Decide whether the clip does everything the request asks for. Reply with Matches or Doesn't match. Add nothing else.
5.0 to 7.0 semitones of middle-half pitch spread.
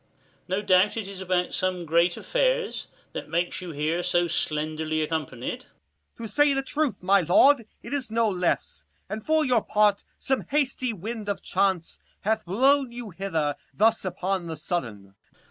Matches